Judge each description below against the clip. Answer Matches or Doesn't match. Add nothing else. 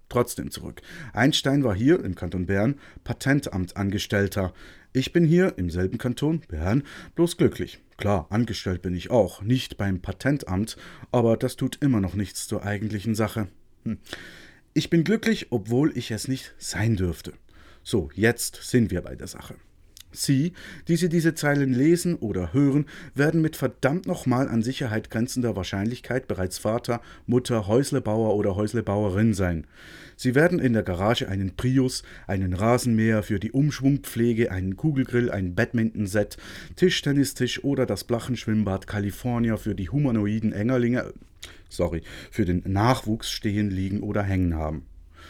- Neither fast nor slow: Matches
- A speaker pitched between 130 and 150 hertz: Doesn't match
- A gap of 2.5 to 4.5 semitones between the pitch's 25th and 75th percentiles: Doesn't match